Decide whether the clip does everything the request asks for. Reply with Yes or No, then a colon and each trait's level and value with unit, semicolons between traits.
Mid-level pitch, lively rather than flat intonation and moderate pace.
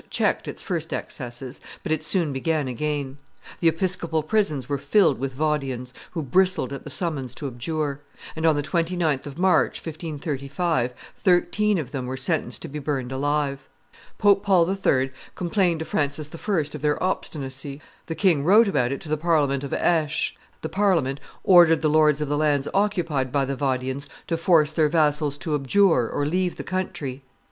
No: medium, 150 Hz; average, 3.7 semitones; average, 175 wpm